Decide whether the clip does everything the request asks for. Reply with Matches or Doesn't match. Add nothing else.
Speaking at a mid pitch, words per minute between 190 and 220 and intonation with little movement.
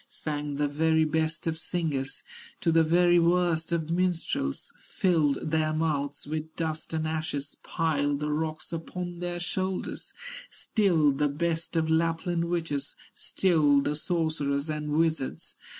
Doesn't match